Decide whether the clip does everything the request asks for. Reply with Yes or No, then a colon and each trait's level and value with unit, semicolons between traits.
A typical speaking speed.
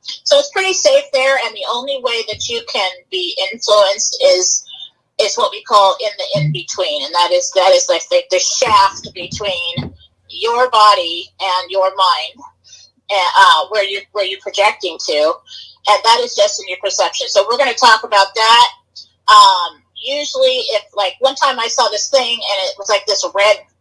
Yes: average, 185 wpm